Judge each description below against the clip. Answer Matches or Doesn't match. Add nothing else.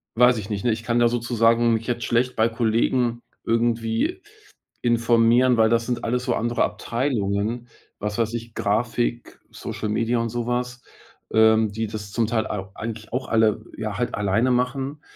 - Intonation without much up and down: Matches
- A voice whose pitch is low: Matches